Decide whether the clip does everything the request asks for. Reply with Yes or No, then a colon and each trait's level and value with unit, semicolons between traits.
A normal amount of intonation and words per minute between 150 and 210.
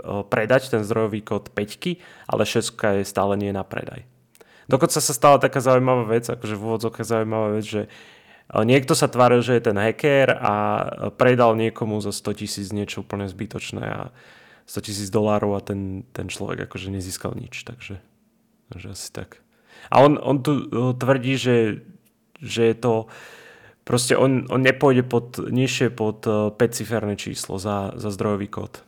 Yes: average, 3.5 semitones; average, 160 wpm